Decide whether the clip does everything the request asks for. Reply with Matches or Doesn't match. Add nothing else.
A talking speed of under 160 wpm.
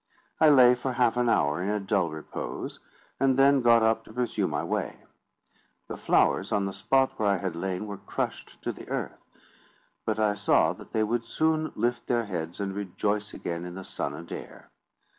Doesn't match